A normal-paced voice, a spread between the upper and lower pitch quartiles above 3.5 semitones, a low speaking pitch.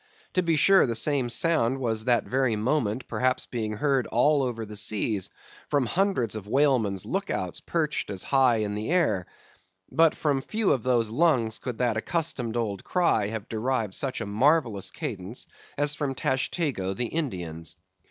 Yes: average, 170 wpm; average, 5.1 semitones; low, 125 Hz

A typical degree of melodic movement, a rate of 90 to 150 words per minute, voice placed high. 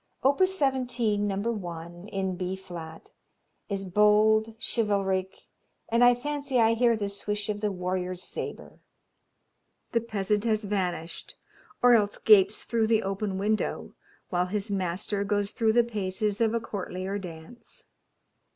Yes: average, 3.0 semitones; average, 140 wpm; high, 205 Hz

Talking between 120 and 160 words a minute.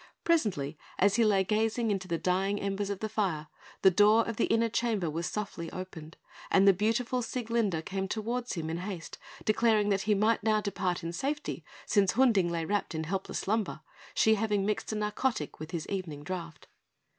No: average, 190 wpm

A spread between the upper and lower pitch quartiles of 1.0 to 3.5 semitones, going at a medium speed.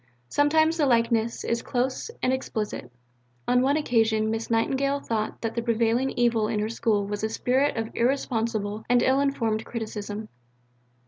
Yes: average, 3.0 semitones; average, 155 wpm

